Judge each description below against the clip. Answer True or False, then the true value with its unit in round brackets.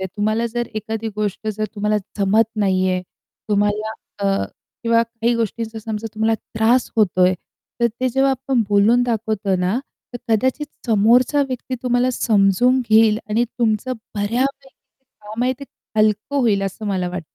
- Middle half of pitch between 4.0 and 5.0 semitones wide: False (2.8 semitones)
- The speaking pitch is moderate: False (220 Hz)